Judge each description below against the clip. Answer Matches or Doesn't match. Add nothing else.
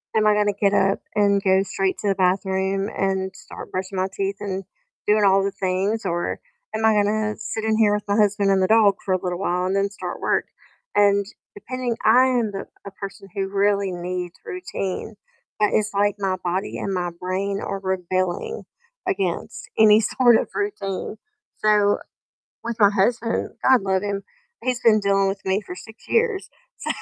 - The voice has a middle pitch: Doesn't match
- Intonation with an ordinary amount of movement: Doesn't match